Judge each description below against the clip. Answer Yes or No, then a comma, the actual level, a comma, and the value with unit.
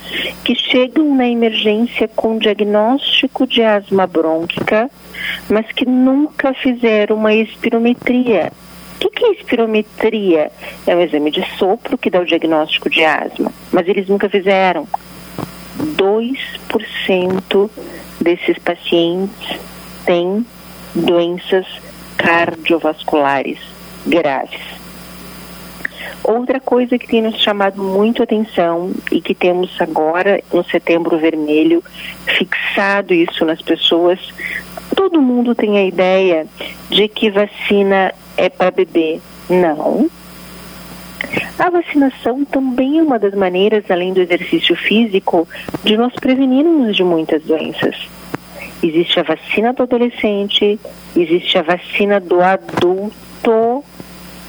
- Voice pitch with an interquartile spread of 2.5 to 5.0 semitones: No, wide, 5.6 semitones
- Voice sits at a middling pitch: No, high, 200 Hz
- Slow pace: Yes, slow, 110 wpm